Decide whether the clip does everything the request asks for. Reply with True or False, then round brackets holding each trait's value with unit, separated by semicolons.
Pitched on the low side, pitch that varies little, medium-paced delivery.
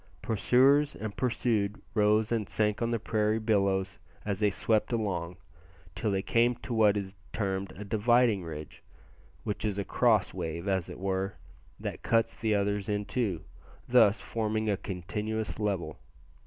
True (105 Hz; 2.3 semitones; 155 wpm)